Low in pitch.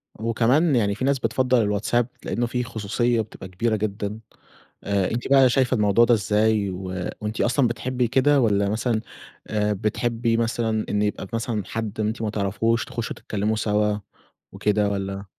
Yes: low, 110 Hz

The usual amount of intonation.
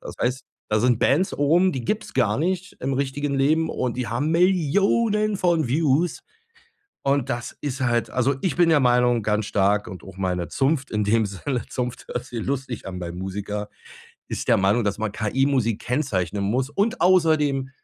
No: wide, 6.0 semitones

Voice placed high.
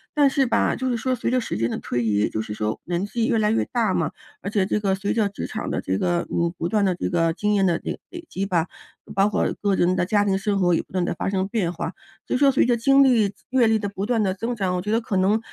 Yes: high, 200 Hz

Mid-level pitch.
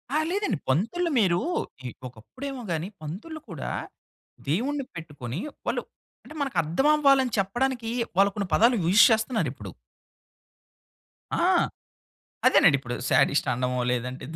No: high, 200 Hz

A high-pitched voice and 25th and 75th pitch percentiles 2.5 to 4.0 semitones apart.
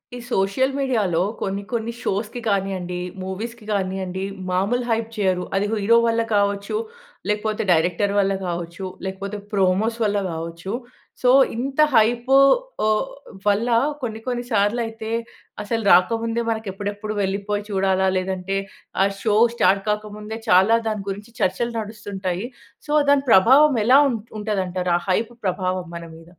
Yes: high, 205 Hz; average, 3.1 semitones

